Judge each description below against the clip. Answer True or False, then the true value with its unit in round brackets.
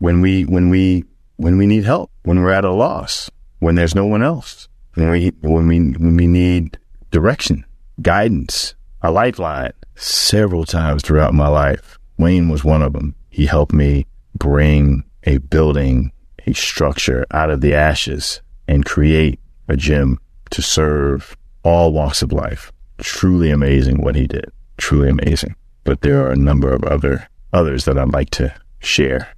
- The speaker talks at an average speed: True (165 wpm)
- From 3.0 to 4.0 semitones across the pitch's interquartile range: True (3.4 semitones)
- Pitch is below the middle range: True (75 Hz)